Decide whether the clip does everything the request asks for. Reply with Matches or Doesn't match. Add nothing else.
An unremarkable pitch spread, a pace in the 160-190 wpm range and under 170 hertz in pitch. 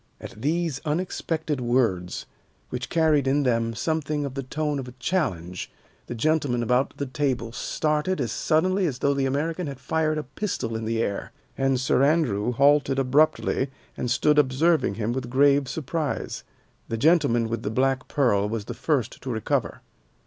Matches